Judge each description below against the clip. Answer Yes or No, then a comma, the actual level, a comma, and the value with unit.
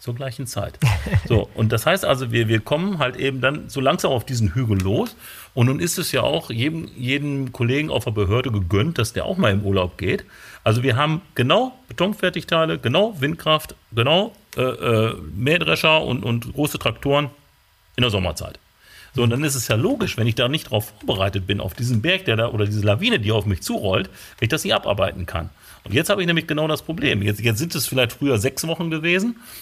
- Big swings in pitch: Yes, wide, 6.0 semitones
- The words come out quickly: Yes, fast, 215 wpm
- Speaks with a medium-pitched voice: No, low, 125 Hz